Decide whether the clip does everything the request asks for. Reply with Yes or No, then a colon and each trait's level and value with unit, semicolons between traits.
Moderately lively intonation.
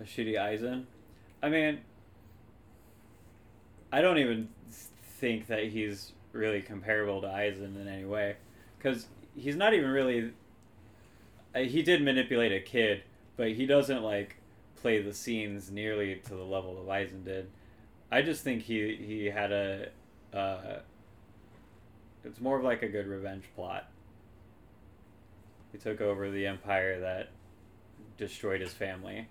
No: narrow, 2.1 semitones